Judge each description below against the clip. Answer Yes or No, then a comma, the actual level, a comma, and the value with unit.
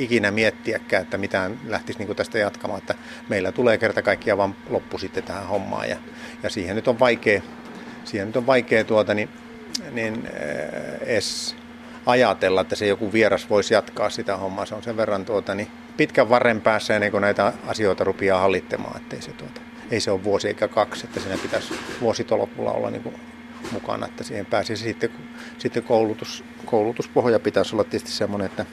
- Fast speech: Yes, fast, 180 wpm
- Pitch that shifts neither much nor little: Yes, average, 3.6 semitones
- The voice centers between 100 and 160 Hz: Yes, low, 110 Hz